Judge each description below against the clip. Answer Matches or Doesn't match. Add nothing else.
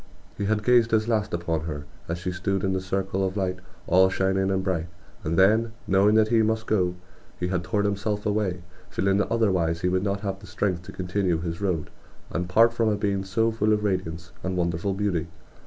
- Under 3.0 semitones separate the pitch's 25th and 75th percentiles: Matches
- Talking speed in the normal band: Doesn't match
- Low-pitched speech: Matches